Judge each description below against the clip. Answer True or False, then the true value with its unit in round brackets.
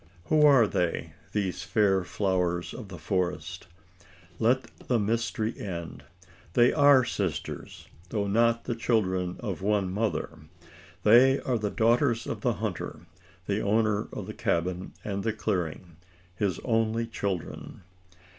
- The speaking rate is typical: False (130 wpm)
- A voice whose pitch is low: True (105 Hz)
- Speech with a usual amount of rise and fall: True (4.0 semitones)